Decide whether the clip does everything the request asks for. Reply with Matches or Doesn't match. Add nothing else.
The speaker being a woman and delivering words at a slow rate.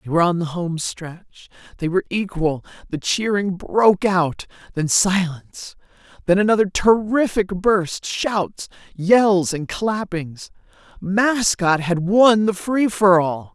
Matches